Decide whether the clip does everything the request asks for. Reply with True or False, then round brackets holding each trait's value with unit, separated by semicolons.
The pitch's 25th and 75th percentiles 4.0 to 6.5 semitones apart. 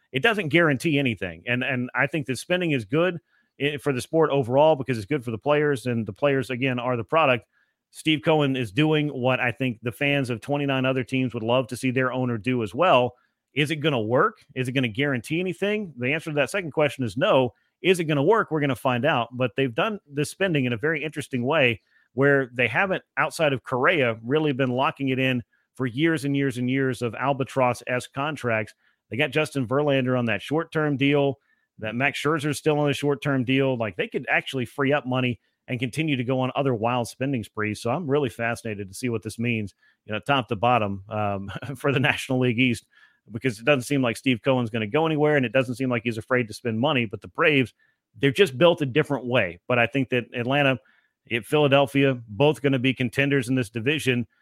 False (3.0 semitones)